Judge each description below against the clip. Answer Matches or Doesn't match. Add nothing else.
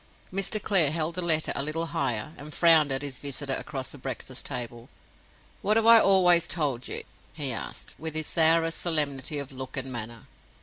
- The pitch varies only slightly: Doesn't match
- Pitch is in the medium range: Matches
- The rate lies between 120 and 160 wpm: Doesn't match